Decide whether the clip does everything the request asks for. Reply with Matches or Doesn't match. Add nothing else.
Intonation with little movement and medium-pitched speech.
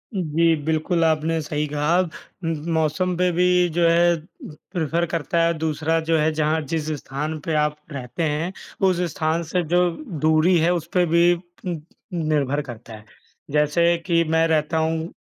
Matches